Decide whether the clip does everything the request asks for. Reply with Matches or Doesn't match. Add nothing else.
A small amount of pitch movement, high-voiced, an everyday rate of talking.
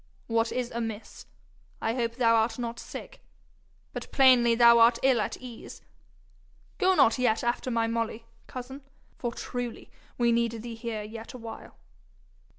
Matches